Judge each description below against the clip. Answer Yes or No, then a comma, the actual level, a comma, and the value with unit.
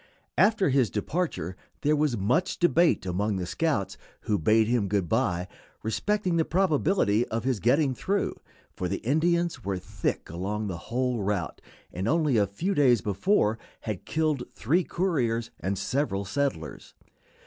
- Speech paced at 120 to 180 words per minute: Yes, average, 150 wpm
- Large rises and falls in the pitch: Yes, wide, 8.0 semitones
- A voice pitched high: No, low, 120 Hz